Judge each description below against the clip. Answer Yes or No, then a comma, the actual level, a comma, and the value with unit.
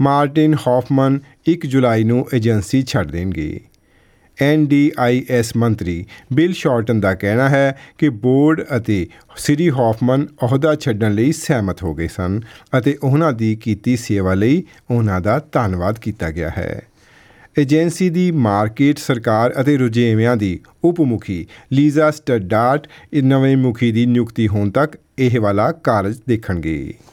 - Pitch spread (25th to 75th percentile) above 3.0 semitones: Yes, average, 5.1 semitones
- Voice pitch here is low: Yes, low, 125 Hz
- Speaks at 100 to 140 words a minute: Yes, slow, 135 wpm